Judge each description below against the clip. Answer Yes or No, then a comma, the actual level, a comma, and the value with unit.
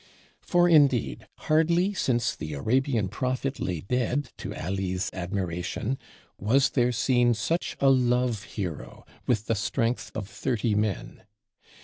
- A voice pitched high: No, low, 120 Hz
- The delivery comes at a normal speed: No, slow, 125 wpm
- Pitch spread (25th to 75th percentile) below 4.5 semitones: No, average, 5.3 semitones